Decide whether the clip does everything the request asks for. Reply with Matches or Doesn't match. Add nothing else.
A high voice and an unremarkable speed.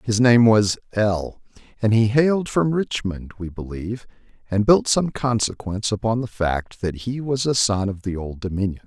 Doesn't match